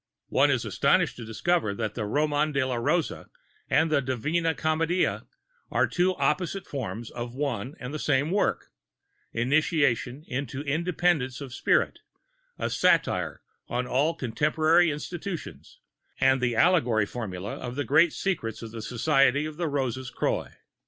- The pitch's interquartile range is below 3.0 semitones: No, average, 4.6 semitones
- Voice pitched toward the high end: No, medium, 140 Hz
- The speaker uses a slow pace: No, average, 145 wpm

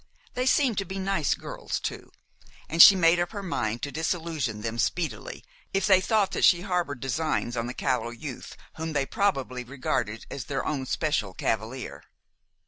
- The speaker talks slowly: No, average, 175 wpm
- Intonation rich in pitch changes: Yes, wide, 6.7 semitones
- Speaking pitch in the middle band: Yes, medium, 155 Hz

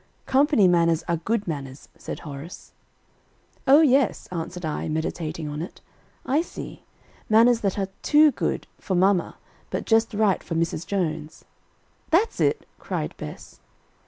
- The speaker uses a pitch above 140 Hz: Yes, medium, 185 Hz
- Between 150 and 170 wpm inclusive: No, average, 140 wpm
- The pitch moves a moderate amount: No, wide, 6.0 semitones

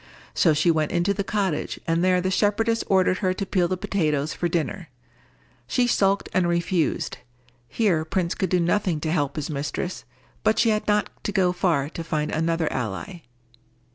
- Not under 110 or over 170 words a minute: No, average, 180 wpm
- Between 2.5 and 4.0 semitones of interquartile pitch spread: Yes, average, 3.5 semitones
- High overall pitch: No, medium, 175 Hz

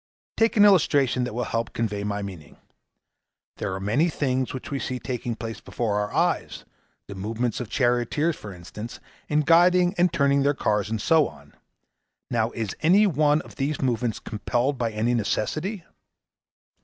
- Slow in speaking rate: No, average, 170 wpm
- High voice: No, low, 125 Hz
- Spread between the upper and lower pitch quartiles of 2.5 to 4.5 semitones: No, wide, 5.5 semitones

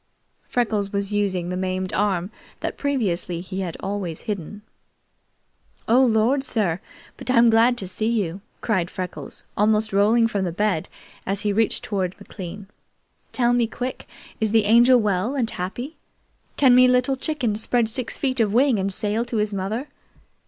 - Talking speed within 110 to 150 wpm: No, average, 165 wpm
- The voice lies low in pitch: No, high, 210 Hz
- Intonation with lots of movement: No, average, 3.9 semitones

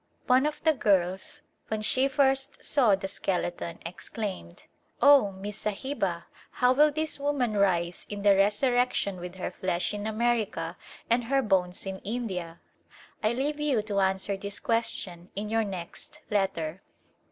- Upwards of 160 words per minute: No, average, 155 wpm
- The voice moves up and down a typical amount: Yes, average, 4.9 semitones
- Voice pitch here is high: Yes, high, 205 Hz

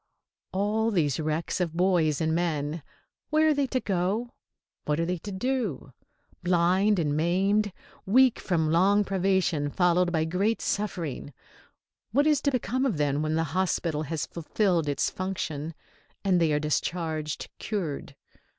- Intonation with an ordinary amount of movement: Yes, average, 4.5 semitones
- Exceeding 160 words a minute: No, average, 150 wpm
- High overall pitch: No, medium, 175 Hz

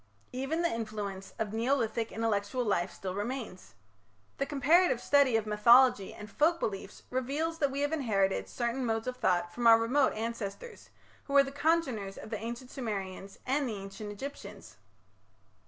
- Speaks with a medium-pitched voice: No, high, 230 Hz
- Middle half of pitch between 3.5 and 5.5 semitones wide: Yes, average, 4.8 semitones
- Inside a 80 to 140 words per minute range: No, average, 160 wpm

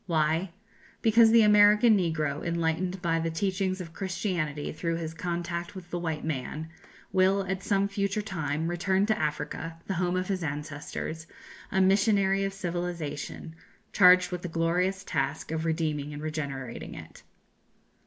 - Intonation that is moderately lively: Yes, average, 3.3 semitones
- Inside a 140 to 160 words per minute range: Yes, average, 150 wpm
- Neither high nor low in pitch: Yes, medium, 175 Hz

